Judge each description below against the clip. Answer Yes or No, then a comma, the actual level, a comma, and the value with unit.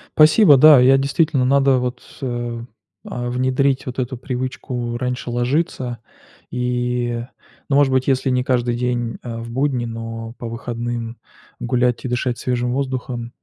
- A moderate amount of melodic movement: No, narrow, 1.6 semitones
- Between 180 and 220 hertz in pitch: No, low, 125 Hz